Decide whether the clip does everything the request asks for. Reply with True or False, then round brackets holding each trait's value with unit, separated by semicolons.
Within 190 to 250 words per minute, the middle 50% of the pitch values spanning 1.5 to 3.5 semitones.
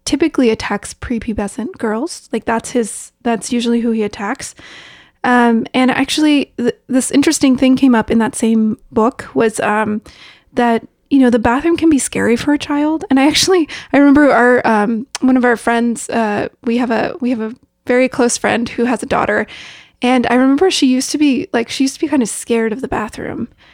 True (205 wpm; 3.1 semitones)